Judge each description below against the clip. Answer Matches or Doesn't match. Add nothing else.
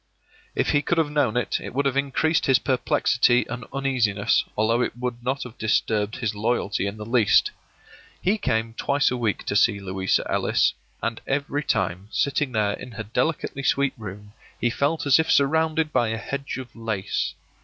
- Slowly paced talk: Doesn't match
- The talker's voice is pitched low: Matches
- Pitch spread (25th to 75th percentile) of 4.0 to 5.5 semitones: Matches